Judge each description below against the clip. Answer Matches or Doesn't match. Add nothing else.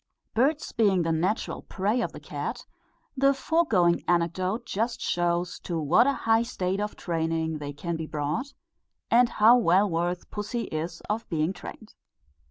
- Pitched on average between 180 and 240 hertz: Matches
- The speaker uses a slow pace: Doesn't match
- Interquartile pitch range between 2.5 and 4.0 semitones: Doesn't match